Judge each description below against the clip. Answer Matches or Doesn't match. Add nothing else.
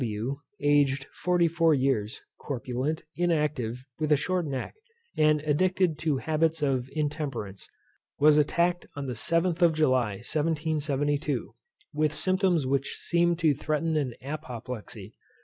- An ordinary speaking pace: Doesn't match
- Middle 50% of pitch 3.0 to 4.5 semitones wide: Matches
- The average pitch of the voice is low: Doesn't match